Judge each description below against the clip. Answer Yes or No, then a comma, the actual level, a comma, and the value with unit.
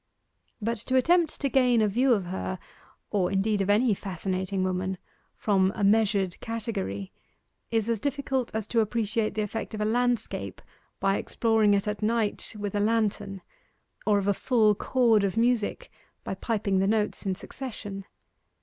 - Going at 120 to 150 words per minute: No, average, 165 wpm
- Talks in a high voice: Yes, high, 210 Hz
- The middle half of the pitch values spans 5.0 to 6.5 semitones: No, average, 2.7 semitones